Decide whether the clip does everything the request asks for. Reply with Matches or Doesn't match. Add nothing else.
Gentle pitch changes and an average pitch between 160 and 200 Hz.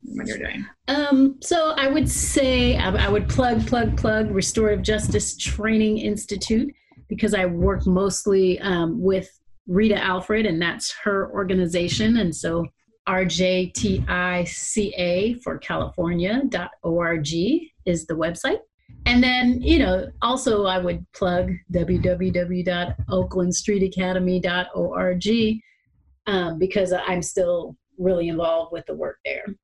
Doesn't match